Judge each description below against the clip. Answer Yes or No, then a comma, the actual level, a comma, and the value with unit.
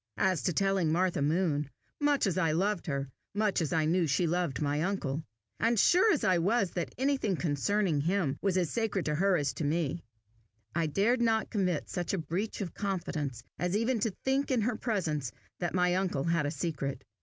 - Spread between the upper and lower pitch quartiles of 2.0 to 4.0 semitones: No, average, 4.8 semitones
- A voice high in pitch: No, medium, 180 Hz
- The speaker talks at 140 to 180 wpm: No, average, 200 wpm